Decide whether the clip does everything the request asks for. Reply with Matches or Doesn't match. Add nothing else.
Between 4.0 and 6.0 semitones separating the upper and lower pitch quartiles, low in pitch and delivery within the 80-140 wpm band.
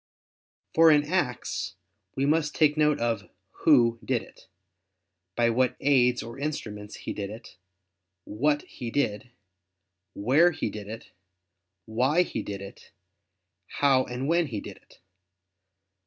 Matches